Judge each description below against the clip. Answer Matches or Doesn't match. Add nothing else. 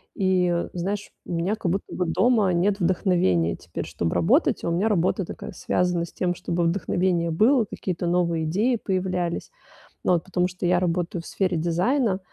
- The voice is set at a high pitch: Doesn't match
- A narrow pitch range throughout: Matches